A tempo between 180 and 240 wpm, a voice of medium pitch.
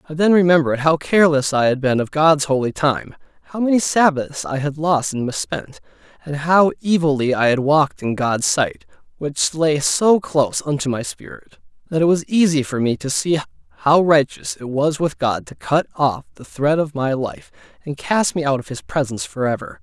Yes: average, 200 wpm; medium, 150 Hz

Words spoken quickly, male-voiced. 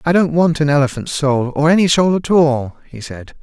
Yes: fast, 230 wpm; male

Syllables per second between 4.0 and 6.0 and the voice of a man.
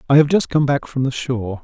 No: 6.2 syllables/s; male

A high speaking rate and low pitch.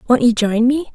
No: fast, 255 wpm; high, 245 Hz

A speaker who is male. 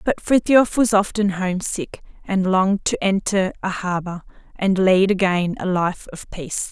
No: female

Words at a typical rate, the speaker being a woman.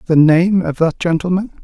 No: average, 185 wpm; male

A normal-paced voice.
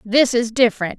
Yes: average, 180 wpm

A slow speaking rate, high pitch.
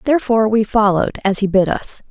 No: average, 200 wpm; high, 210 Hz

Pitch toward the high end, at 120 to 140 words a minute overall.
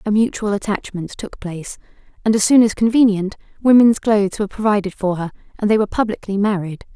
No: high, 205 Hz; average, 180 wpm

